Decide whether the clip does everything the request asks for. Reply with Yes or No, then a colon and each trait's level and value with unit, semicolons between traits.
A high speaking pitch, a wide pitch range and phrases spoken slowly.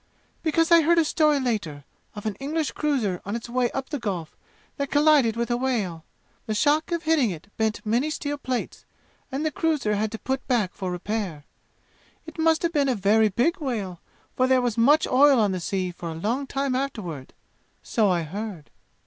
No: high, 240 Hz; wide, 6.2 semitones; average, 200 wpm